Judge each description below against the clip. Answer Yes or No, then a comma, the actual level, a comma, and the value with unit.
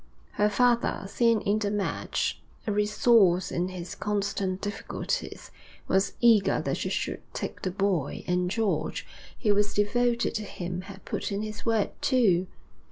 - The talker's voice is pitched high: Yes, high, 205 Hz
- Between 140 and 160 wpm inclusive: Yes, average, 155 wpm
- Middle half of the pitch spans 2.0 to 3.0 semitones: Yes, narrow, 2.6 semitones